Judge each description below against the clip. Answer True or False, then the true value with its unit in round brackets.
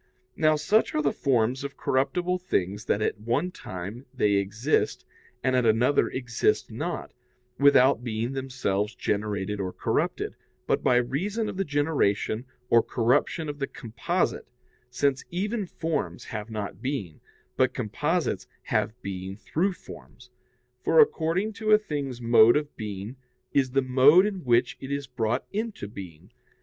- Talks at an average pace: True (150 wpm)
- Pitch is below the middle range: True (130 Hz)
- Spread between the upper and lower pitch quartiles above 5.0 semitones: True (5.6 semitones)